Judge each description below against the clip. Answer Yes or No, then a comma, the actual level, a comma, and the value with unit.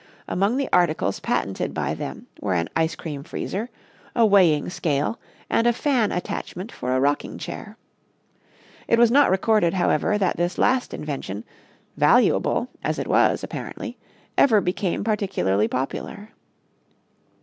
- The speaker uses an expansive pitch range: Yes, wide, 6.9 semitones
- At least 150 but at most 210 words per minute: No, average, 140 wpm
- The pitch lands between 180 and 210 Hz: Yes, medium, 185 Hz